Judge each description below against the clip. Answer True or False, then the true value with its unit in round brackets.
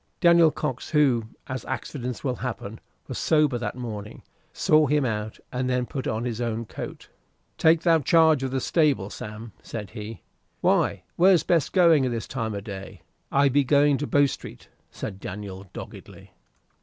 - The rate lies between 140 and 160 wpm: False (170 wpm)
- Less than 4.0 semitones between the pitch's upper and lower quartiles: False (5.1 semitones)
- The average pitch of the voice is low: True (125 Hz)